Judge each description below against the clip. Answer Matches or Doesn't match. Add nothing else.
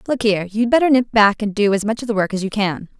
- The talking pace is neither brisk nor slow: Doesn't match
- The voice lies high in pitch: Matches